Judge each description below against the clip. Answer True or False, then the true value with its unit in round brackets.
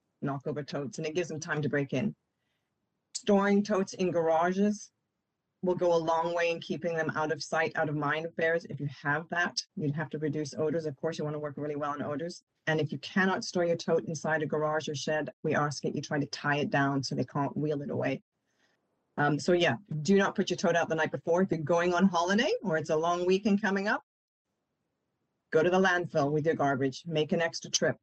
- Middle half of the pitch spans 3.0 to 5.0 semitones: False (2.6 semitones)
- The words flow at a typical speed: False (240 wpm)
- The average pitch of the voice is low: False (160 Hz)